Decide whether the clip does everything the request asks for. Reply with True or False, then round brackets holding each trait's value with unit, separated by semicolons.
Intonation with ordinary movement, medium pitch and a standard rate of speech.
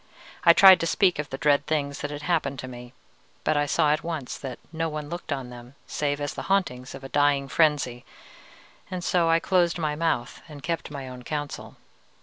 False (3.4 semitones; 145 Hz; 210 wpm)